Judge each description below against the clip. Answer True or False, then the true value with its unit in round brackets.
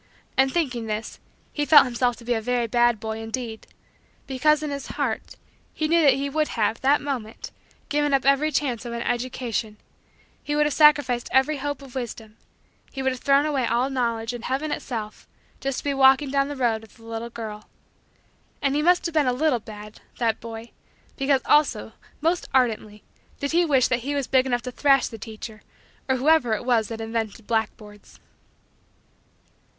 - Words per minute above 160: True (190 wpm)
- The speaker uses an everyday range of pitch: True (3.8 semitones)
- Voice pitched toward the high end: True (255 Hz)